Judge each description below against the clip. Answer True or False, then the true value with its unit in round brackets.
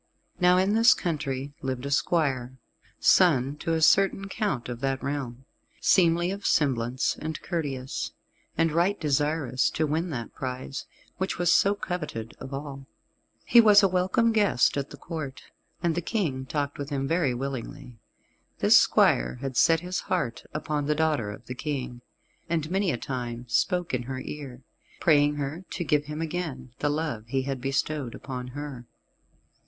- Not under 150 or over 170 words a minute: True (165 wpm)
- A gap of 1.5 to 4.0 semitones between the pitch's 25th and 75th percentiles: False (4.5 semitones)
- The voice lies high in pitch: False (145 Hz)